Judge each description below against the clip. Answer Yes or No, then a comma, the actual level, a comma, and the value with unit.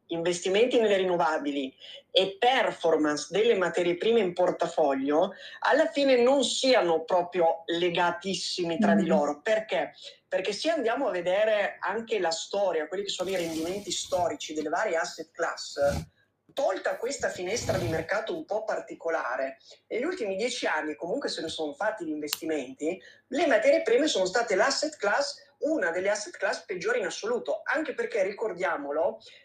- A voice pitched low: No, medium, 180 Hz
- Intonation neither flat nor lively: No, wide, 6.7 semitones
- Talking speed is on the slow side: No, average, 150 wpm